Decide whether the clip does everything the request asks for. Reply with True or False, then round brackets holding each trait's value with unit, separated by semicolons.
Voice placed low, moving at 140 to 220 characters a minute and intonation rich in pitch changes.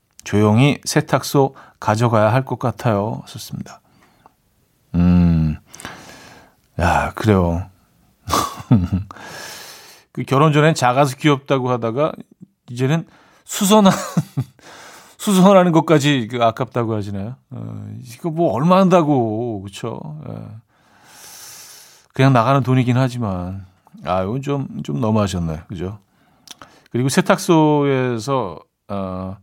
True (125 Hz; 215 characters per minute; 6.0 semitones)